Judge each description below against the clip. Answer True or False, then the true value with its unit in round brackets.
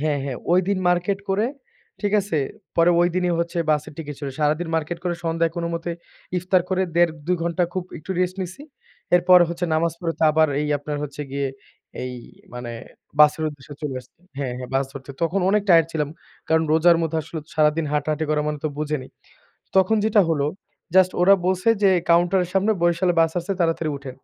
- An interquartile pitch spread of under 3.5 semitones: True (3.1 semitones)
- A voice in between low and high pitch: True (165 Hz)